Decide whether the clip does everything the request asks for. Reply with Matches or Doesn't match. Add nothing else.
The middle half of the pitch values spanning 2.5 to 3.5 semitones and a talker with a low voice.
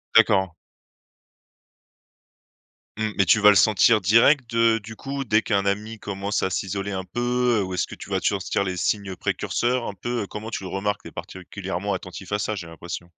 Matches